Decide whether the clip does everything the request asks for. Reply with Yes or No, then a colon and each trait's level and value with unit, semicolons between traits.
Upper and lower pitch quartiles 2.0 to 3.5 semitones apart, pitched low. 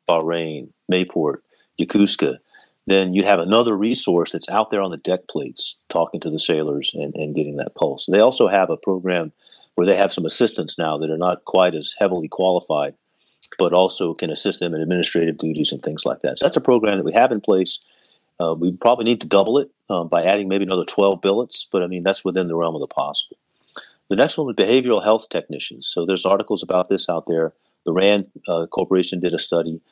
Yes: average, 2.8 semitones; very low, 90 Hz